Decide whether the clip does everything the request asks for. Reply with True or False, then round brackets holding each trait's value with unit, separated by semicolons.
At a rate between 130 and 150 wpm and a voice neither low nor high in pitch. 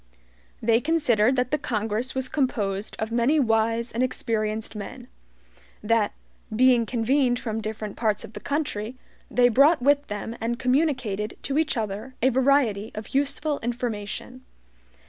False (145 wpm; 235 Hz)